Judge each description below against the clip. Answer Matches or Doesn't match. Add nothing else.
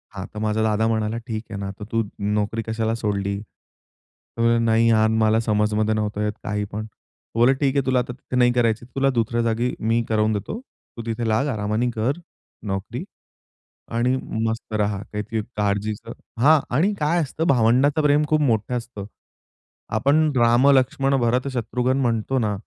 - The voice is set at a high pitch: Doesn't match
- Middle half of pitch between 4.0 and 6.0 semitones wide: Doesn't match